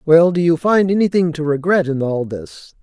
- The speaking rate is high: Yes, fast, 215 wpm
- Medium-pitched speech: Yes, medium, 165 Hz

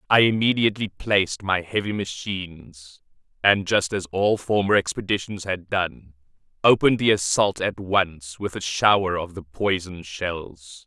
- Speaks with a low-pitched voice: Yes, very low, 95 Hz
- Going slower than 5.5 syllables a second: Yes, 4.4 syllables/s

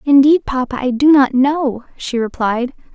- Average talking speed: Yes, average, 165 wpm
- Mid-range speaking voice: No, very high, 265 Hz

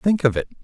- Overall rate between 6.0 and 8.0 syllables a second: Yes, 6.5 syllables/s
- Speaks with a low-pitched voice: No, medium, 145 Hz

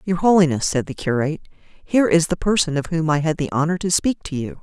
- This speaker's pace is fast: Yes, fast, 245 wpm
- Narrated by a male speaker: No, female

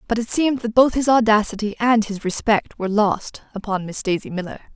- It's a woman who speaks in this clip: Yes, female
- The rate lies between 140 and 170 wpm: No, average, 200 wpm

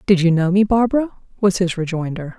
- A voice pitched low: No, high, 190 Hz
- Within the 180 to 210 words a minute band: Yes, average, 200 wpm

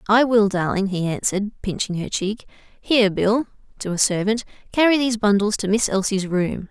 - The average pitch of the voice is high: Yes, high, 210 Hz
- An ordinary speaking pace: Yes, average, 160 wpm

